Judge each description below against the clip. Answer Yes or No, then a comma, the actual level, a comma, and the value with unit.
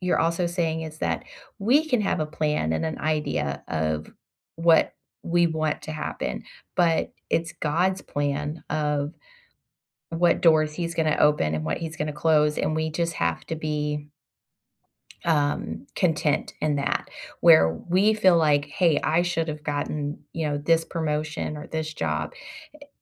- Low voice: No, medium, 155 Hz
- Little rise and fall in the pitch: Yes, narrow, 2.1 semitones